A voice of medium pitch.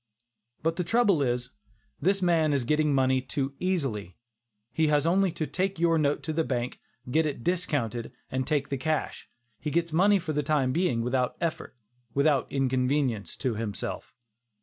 Yes: medium, 150 Hz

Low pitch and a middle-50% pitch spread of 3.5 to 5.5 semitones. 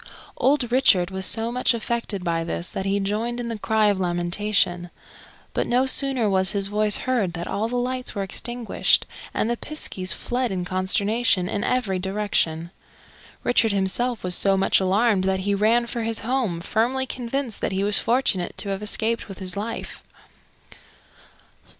No: high, 210 Hz; average, 4.0 semitones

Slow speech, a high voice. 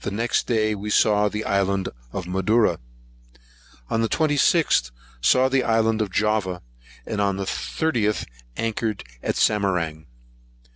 No: slow, 130 wpm; low, 105 Hz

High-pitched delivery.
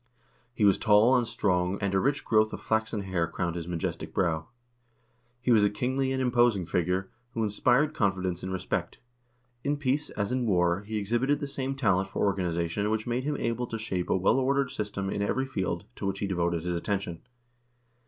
No: low, 105 Hz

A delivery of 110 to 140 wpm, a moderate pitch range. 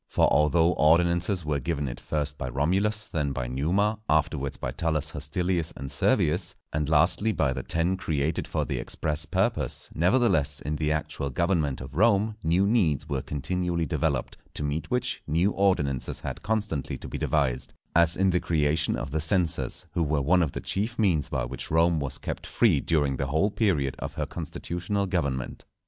No: average, 180 wpm; average, 4.0 semitones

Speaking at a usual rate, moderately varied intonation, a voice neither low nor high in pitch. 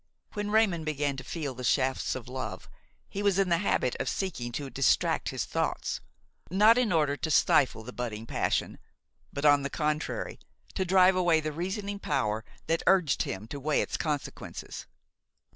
No: average, 175 wpm; wide, 6.1 semitones; medium, 155 Hz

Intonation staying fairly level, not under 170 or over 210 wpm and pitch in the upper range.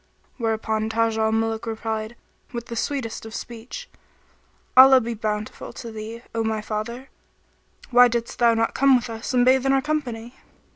Yes: narrow, 2.0 semitones; average, 180 wpm; high, 230 Hz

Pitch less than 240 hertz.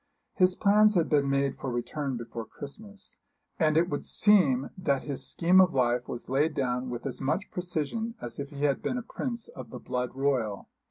Yes: medium, 140 Hz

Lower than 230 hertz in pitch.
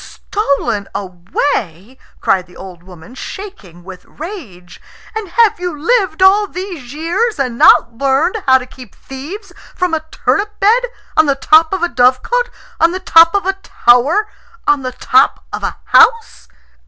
No: very high, 310 Hz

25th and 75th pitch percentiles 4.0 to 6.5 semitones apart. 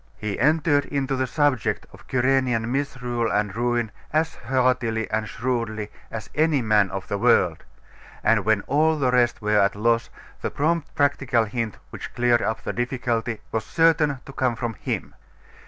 No: average, 3.5 semitones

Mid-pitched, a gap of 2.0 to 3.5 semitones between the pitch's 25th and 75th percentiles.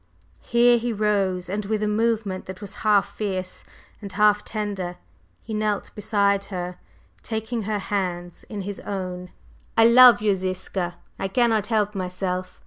No: high, 205 Hz; narrow, 2.5 semitones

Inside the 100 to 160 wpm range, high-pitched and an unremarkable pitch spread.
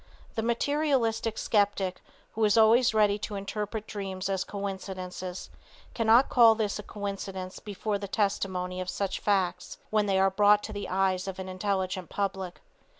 No: average, 155 wpm; high, 200 Hz; narrow, 2.3 semitones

